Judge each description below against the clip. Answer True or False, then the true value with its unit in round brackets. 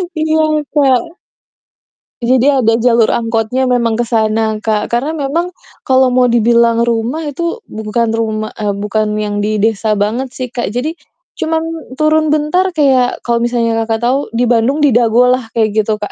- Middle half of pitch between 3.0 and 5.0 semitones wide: True (3.6 semitones)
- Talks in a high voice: True (240 Hz)